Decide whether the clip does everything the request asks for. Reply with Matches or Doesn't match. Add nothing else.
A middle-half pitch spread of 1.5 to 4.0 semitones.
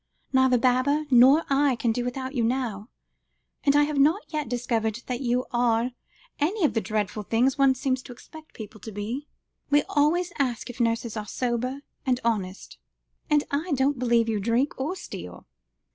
Matches